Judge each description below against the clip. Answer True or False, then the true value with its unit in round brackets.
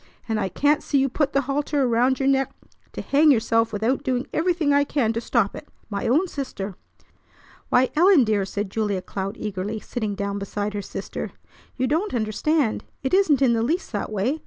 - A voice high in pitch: True (245 Hz)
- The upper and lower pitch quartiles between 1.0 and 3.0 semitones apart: False (5.3 semitones)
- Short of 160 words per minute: False (190 wpm)